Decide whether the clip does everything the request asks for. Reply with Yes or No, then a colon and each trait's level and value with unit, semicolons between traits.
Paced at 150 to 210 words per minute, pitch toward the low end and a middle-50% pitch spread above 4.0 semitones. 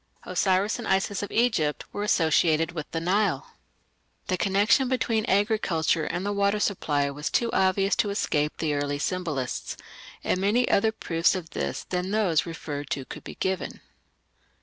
No: average, 160 wpm; medium, 185 Hz; average, 4.4 semitones